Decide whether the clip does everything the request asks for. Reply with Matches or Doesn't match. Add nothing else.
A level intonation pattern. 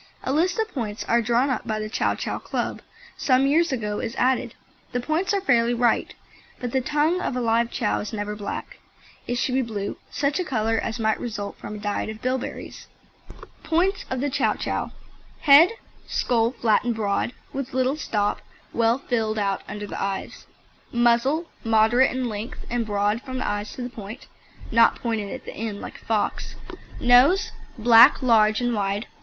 Doesn't match